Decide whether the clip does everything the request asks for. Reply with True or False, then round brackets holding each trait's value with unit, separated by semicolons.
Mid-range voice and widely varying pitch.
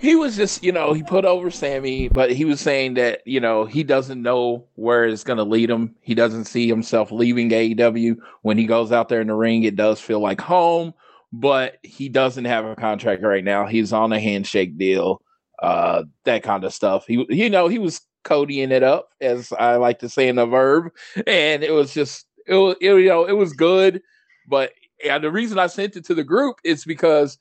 False (130 Hz; 7.5 semitones)